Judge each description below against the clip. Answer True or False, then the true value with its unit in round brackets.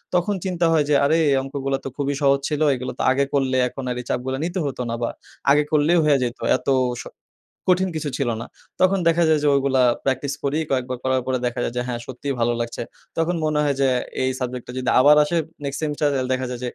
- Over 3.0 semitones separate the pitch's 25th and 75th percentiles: False (2.7 semitones)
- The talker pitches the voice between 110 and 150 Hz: True (140 Hz)